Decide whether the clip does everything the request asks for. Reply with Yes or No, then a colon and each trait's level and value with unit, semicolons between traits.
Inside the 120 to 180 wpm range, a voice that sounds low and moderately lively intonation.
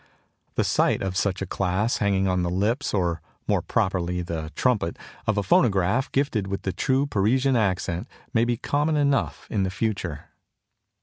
Yes: average, 170 wpm; low, 100 Hz; average, 4.7 semitones